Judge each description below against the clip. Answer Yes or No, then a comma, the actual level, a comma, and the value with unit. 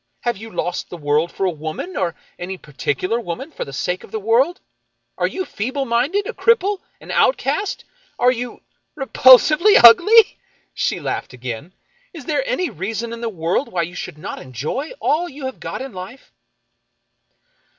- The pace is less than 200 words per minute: Yes, average, 180 wpm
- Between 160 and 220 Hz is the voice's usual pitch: No, high, 235 Hz